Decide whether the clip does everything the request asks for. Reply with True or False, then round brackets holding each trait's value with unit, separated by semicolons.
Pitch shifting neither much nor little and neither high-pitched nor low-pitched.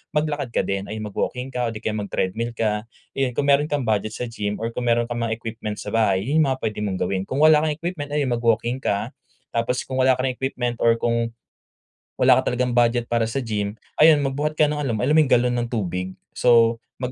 False (3.3 semitones; 120 Hz)